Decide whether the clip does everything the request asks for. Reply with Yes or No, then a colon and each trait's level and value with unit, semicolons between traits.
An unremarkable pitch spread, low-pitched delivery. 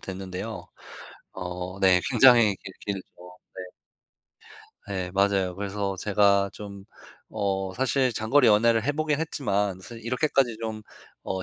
Yes: average, 3.5 semitones; low, 100 Hz